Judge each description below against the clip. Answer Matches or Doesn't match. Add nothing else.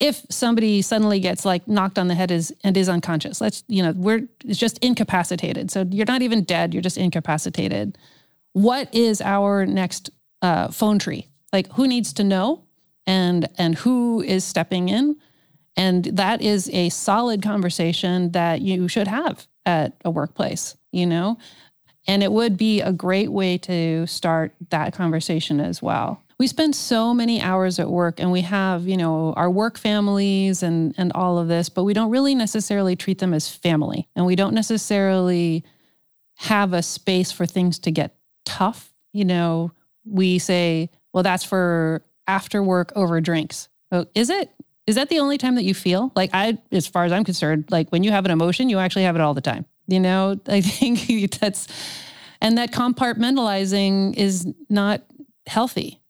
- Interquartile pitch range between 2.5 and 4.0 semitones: Matches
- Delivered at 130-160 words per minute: Doesn't match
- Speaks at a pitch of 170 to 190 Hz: Matches